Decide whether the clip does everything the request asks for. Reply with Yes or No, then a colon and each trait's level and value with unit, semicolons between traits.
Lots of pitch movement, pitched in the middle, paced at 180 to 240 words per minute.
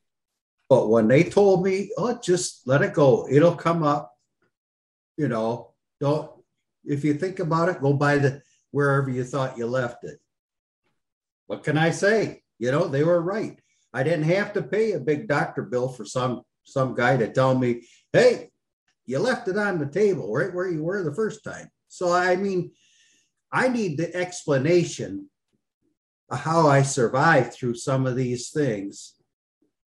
No: wide, 5.9 semitones; medium, 150 Hz; average, 170 wpm